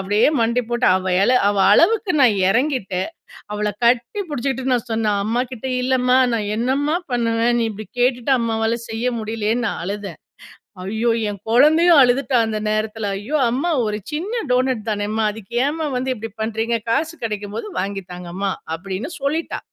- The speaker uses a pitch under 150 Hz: No, high, 230 Hz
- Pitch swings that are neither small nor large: Yes, average, 3.6 semitones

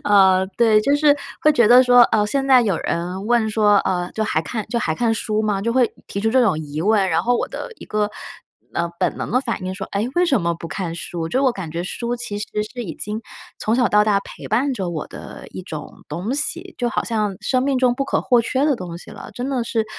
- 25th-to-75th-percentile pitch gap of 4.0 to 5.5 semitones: Yes, average, 4.7 semitones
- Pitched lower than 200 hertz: No, high, 215 Hz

